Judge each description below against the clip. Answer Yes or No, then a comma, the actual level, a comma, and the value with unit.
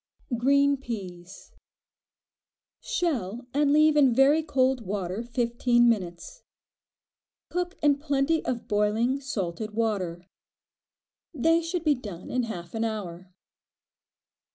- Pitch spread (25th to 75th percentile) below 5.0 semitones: No, wide, 5.5 semitones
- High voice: Yes, high, 240 Hz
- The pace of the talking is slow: Yes, slow, 105 wpm